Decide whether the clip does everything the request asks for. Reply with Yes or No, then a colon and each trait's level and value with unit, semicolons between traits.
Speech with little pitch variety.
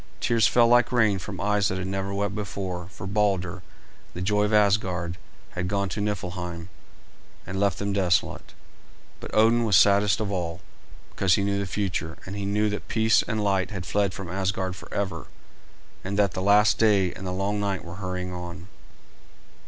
Yes: narrow, 2.1 semitones